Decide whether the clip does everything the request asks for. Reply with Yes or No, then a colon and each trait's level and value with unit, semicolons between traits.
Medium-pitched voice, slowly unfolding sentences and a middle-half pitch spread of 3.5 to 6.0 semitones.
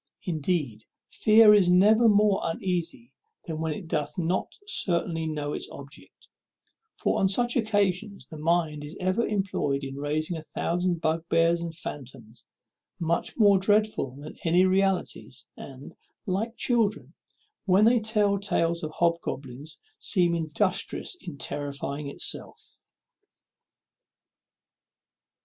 Yes: medium, 170 Hz; slow, 120 wpm; average, 4.8 semitones